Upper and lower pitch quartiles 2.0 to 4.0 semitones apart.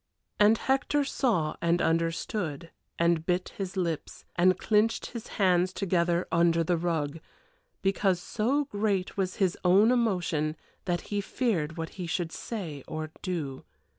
Yes: average, 3.7 semitones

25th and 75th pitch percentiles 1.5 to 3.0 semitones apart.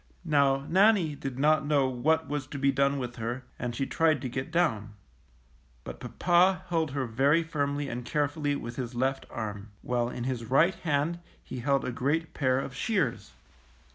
No: average, 3.7 semitones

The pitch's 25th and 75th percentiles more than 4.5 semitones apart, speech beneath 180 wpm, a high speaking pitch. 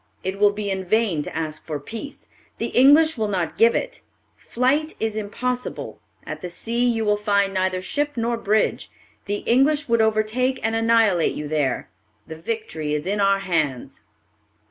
No: average, 4.1 semitones; average, 170 wpm; high, 215 Hz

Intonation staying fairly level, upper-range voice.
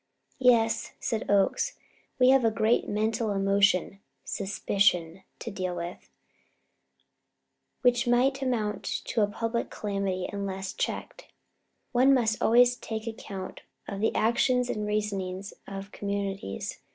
No: average, 3.2 semitones; high, 210 Hz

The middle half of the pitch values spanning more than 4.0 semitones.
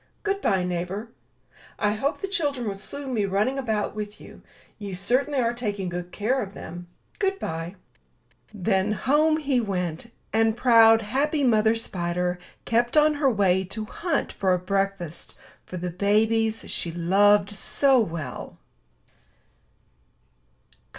Yes: average, 5.1 semitones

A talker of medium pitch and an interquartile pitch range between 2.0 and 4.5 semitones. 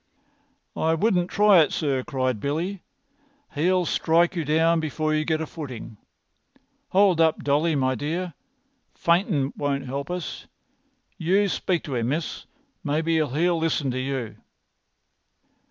Yes: medium, 160 Hz; average, 3.6 semitones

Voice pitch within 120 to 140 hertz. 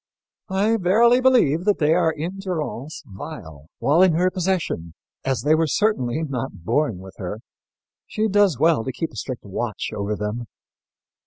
No: medium, 155 Hz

